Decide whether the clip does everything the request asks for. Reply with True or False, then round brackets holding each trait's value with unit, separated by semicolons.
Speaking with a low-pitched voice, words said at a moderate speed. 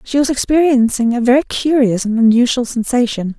False (245 Hz; 160 wpm)